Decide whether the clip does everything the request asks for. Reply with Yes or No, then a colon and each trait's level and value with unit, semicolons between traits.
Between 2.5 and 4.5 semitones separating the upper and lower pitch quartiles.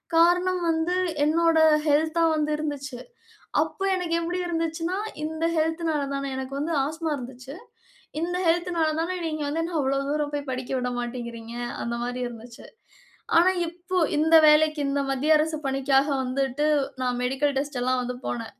Yes: average, 3.9 semitones